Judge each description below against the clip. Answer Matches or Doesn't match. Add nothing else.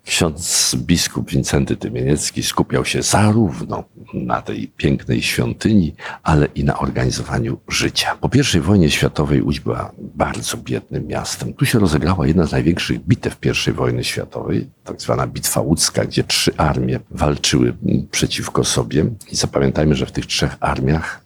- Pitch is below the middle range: Matches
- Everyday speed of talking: Matches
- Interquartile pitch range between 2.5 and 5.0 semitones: Doesn't match